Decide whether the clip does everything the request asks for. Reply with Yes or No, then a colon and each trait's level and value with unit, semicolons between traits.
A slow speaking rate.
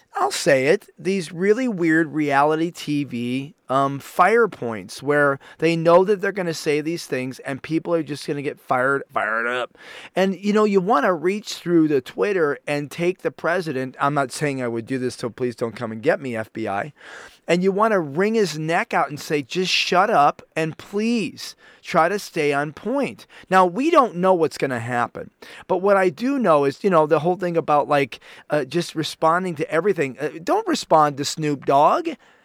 No: average, 200 wpm